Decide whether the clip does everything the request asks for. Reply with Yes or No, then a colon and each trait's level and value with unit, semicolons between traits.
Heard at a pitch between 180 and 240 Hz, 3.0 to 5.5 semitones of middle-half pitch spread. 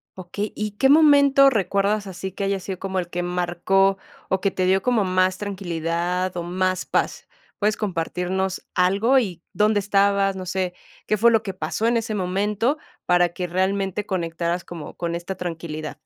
No: high, 190 Hz; narrow, 2.5 semitones